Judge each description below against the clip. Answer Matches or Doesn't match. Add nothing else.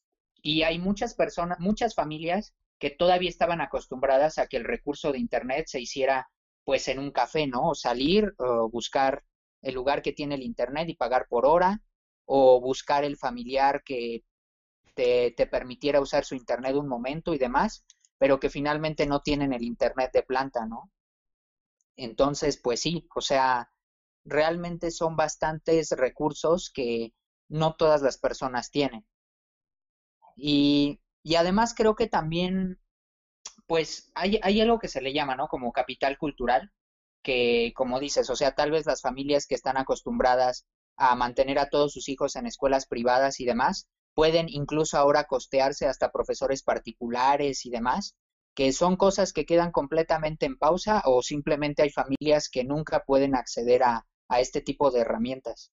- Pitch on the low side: Doesn't match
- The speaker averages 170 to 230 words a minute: Doesn't match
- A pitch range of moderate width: Matches